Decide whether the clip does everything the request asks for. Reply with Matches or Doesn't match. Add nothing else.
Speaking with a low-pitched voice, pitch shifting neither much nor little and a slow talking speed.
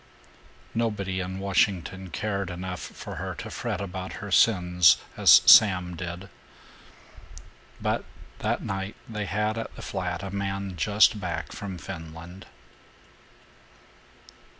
Doesn't match